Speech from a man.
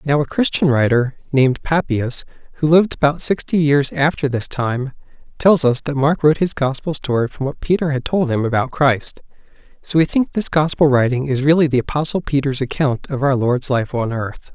Yes: male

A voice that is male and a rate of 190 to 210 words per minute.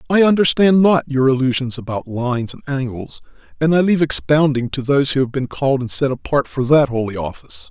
Yes: male; average, 200 wpm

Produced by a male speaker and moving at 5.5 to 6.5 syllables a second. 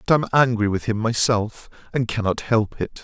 No: male; 5.3 syllables/s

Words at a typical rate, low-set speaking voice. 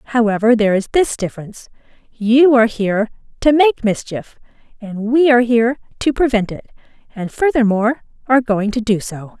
No: average, 160 wpm; high, 230 Hz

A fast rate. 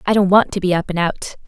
Yes: fast, 325 wpm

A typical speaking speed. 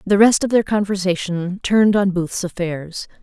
Yes: average, 170 wpm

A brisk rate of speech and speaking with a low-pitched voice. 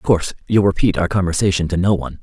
Yes: fast, 245 wpm; very low, 90 Hz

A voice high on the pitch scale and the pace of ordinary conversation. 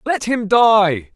Yes: high, 200 Hz; average, 155 wpm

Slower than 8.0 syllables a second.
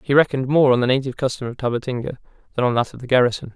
No: 8.1 syllables/s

